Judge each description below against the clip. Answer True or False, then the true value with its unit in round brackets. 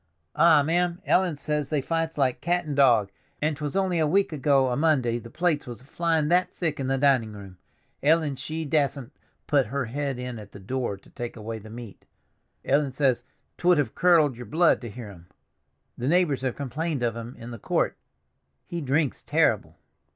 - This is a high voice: False (140 Hz)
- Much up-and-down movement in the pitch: False (4.8 semitones)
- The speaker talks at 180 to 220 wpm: True (195 wpm)